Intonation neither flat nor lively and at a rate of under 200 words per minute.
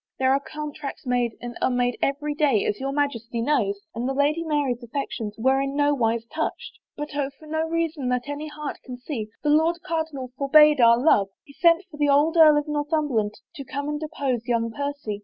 No: average, 3.5 semitones; fast, 205 wpm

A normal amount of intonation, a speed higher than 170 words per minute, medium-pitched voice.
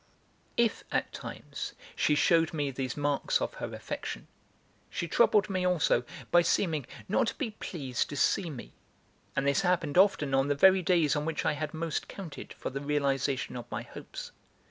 Yes: average, 4.4 semitones; average, 180 wpm; medium, 150 Hz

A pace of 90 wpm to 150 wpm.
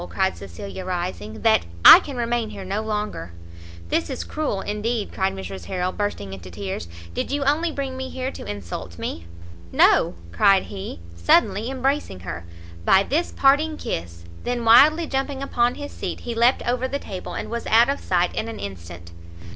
No: average, 180 wpm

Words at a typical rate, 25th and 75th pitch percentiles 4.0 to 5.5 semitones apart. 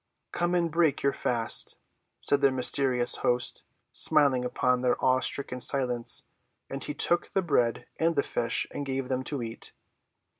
No: average, 155 wpm; narrow, 2.6 semitones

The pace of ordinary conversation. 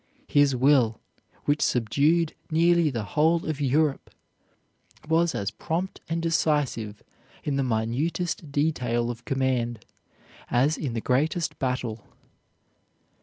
No: slow, 115 wpm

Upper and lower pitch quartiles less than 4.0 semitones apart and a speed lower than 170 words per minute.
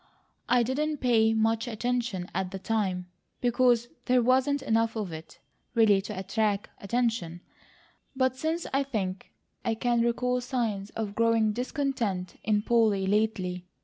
Yes: average, 3.6 semitones; average, 140 wpm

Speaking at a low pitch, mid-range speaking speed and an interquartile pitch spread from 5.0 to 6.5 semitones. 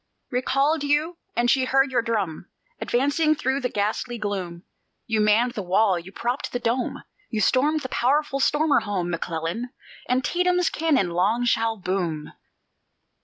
No: high, 240 Hz; average, 145 wpm; average, 5.3 semitones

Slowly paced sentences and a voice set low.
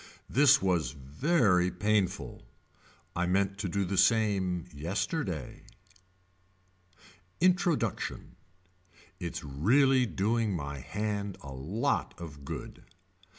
Yes: slow, 95 wpm; very low, 95 Hz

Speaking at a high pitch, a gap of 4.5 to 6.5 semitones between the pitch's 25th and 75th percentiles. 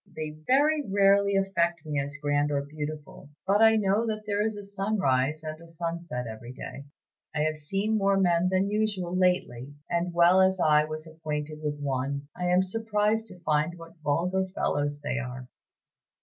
No: medium, 170 Hz; average, 4.8 semitones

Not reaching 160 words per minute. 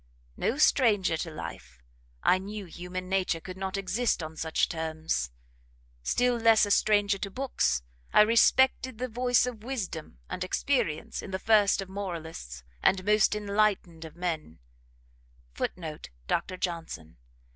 Yes: average, 140 wpm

